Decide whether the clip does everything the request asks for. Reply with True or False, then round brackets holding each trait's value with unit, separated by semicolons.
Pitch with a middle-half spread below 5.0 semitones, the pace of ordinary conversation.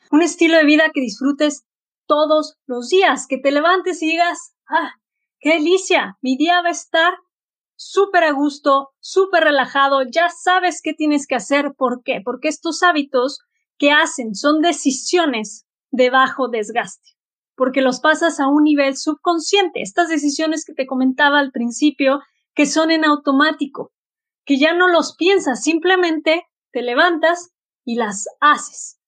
True (3.9 semitones; 155 wpm)